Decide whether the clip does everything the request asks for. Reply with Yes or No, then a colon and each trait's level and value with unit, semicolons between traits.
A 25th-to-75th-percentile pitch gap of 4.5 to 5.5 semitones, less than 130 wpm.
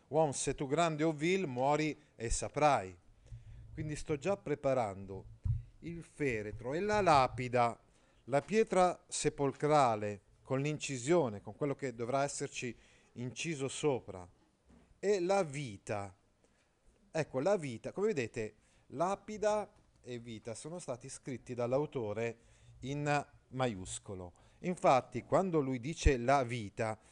Yes: average, 4.9 semitones; slow, 115 wpm